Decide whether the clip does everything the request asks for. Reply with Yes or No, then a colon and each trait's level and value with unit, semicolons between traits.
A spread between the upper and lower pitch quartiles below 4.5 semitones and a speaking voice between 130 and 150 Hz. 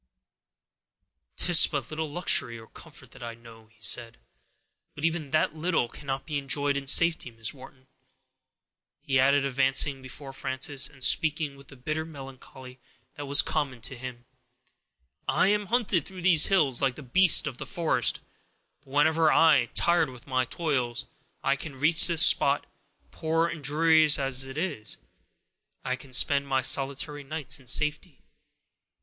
Yes: average, 3.3 semitones; medium, 140 Hz